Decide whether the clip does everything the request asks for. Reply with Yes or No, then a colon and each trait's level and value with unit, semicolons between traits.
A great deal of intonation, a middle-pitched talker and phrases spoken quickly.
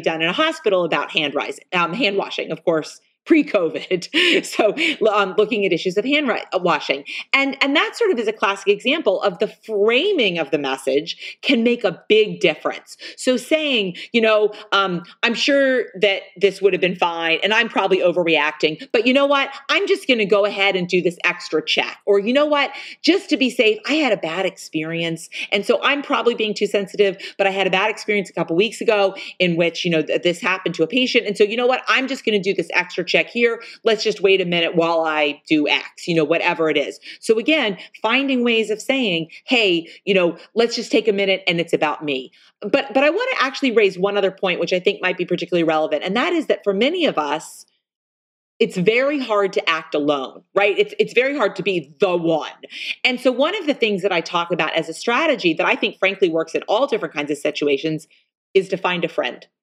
No: wide, 6.6 semitones; high, 200 Hz; fast, 230 wpm